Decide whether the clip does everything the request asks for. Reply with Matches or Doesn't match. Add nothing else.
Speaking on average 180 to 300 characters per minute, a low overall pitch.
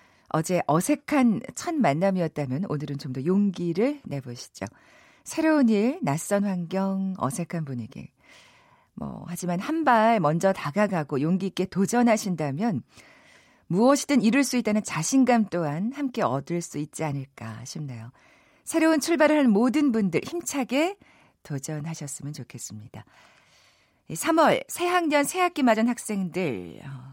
Doesn't match